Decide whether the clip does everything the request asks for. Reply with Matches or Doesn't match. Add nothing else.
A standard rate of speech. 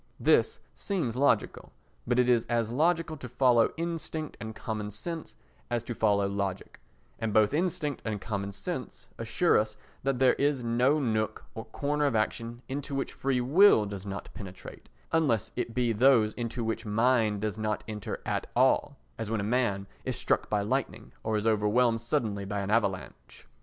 Matches